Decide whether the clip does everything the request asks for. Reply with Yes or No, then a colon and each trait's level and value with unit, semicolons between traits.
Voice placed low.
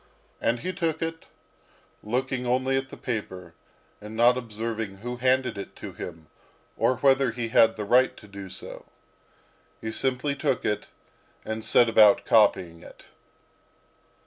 Yes: low, 120 Hz